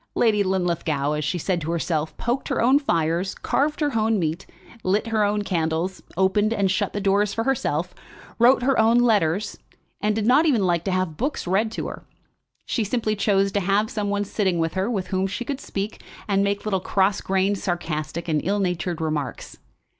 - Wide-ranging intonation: No, average, 3.8 semitones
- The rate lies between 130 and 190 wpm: No, average, 200 wpm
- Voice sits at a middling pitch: No, high, 195 Hz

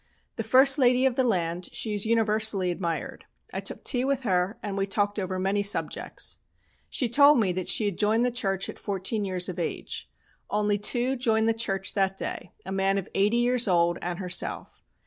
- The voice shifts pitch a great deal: No, average, 3.6 semitones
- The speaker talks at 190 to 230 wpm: Yes, average, 200 wpm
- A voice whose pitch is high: Yes, high, 205 Hz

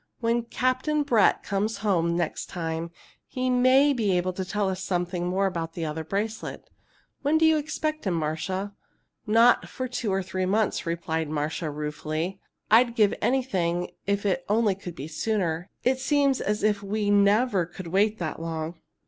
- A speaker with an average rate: Yes, average, 170 wpm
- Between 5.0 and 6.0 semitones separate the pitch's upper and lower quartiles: Yes, average, 5.3 semitones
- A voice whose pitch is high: Yes, high, 195 Hz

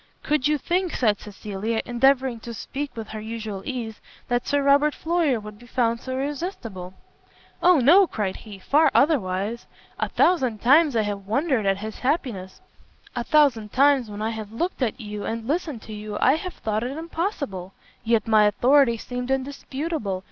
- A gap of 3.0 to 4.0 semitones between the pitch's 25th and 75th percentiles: No, average, 5.1 semitones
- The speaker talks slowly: No, average, 175 wpm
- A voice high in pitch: Yes, high, 240 Hz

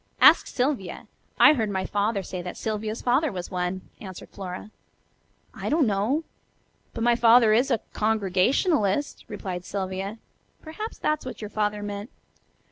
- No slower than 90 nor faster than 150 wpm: Yes, average, 145 wpm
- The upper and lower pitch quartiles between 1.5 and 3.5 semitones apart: No, average, 4.2 semitones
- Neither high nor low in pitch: No, high, 210 Hz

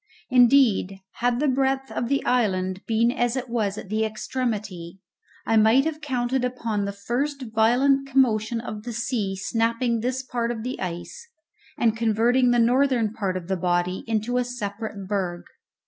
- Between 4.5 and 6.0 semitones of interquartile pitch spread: No, average, 3.3 semitones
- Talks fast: No, average, 165 wpm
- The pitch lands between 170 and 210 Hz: No, high, 230 Hz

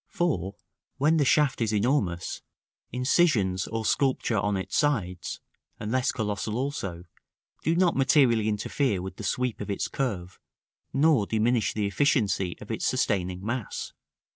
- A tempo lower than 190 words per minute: Yes, average, 140 wpm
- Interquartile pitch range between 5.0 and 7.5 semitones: Yes, wide, 5.5 semitones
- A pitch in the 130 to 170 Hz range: No, low, 110 Hz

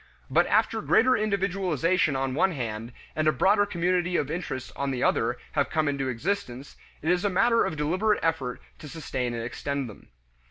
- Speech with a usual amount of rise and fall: No, wide, 6.0 semitones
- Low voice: No, medium, 155 Hz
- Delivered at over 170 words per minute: Yes, average, 185 wpm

